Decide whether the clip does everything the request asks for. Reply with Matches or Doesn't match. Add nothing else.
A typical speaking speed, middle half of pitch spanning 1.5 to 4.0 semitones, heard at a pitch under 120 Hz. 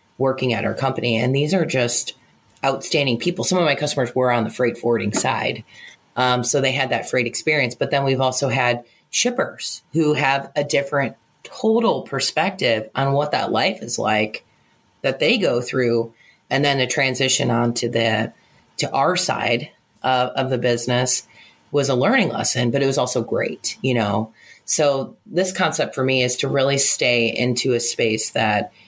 Doesn't match